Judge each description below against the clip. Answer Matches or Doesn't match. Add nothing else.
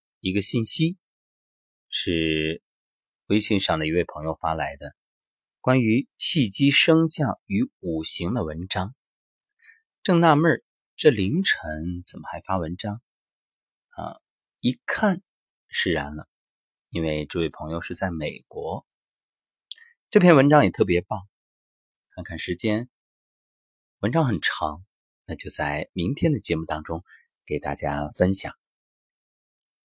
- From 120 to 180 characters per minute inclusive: Matches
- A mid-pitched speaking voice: Doesn't match